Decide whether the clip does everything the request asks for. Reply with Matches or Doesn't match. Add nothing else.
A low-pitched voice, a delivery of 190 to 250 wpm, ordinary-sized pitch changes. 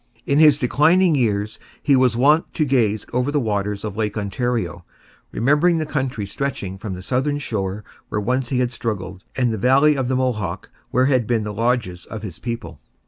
Matches